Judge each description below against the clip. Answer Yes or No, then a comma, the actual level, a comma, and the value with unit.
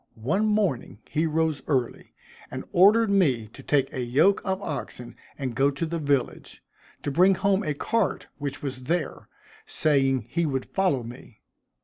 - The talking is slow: No, average, 160 wpm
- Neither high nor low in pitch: Yes, medium, 150 Hz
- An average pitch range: No, wide, 6.1 semitones